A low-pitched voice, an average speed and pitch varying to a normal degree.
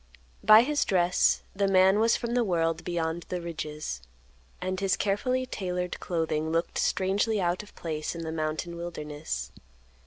No: medium, 175 Hz; average, 155 wpm; average, 3.4 semitones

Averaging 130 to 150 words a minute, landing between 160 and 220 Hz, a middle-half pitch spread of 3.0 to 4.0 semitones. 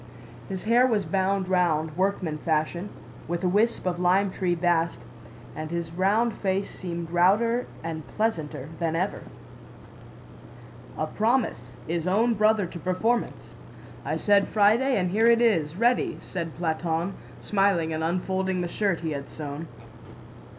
Yes: average, 145 wpm; medium, 185 Hz; average, 3.7 semitones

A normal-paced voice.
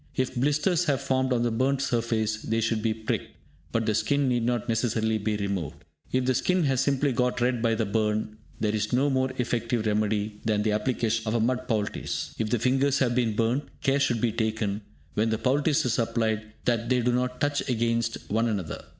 No: fast, 210 wpm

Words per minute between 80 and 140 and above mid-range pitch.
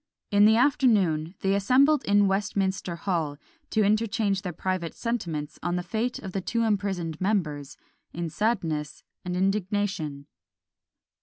Yes: slow, 135 wpm; high, 195 Hz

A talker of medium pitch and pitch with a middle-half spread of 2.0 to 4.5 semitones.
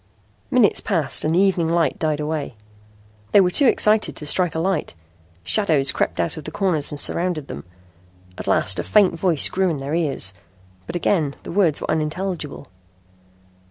Yes: medium, 165 Hz; average, 4.0 semitones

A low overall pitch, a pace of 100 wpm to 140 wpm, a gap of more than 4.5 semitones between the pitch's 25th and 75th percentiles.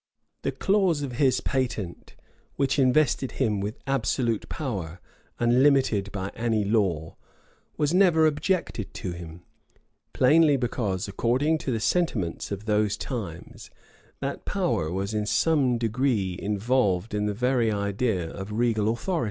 Yes: low, 115 Hz; slow, 135 wpm; average, 5.2 semitones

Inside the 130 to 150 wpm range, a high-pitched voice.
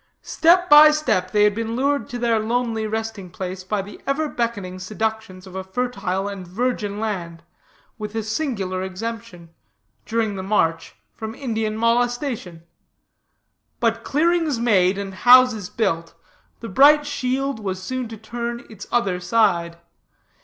Yes: average, 145 wpm; high, 220 Hz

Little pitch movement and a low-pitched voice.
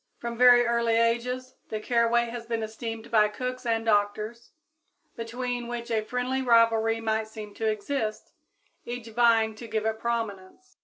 No: narrow, 1.5 semitones; high, 230 Hz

